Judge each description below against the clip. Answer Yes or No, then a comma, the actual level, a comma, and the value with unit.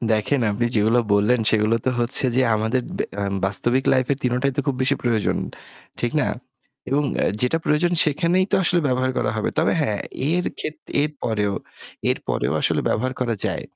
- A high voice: No, low, 125 Hz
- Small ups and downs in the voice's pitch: No, average, 4.6 semitones